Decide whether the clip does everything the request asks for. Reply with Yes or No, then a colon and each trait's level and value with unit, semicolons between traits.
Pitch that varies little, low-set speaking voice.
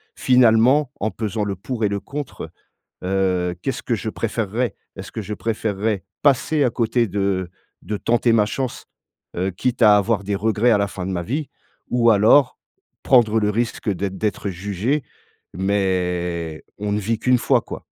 No: average, 3.5 semitones; low, 105 Hz